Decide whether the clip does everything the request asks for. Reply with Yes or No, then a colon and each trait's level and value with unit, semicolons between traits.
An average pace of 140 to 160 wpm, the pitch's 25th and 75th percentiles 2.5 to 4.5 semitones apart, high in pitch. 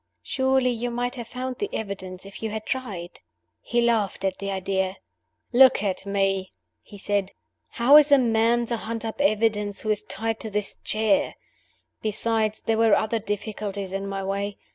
No: average, 175 wpm; average, 3.0 semitones; high, 215 Hz